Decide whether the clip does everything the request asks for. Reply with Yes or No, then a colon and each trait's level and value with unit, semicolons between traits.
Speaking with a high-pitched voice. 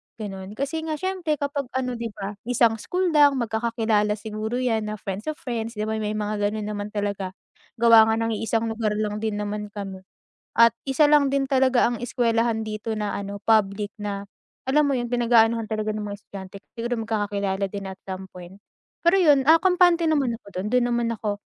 Yes: high, 220 Hz